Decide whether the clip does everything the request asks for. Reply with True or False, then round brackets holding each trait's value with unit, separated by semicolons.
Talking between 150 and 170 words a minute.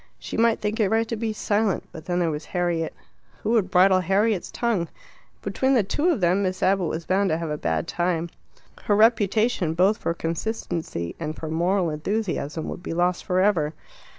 False (195 wpm)